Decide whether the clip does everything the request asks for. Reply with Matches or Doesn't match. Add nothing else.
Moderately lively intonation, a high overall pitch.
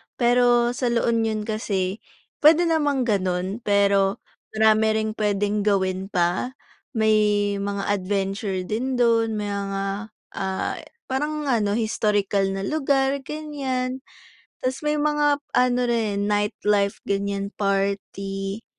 Matches